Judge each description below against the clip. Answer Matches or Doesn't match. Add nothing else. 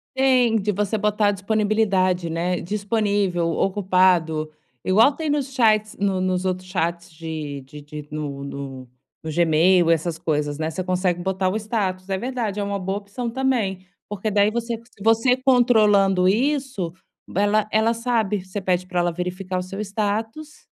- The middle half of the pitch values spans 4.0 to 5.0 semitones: Doesn't match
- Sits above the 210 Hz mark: Doesn't match